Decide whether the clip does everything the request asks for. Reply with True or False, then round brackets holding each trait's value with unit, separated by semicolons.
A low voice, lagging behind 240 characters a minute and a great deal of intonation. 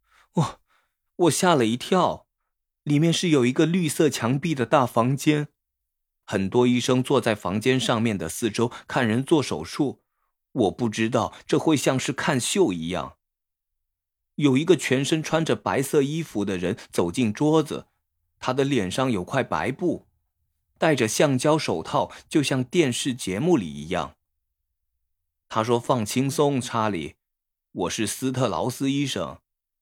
True (125 Hz; 210 characters per minute; 7.3 semitones)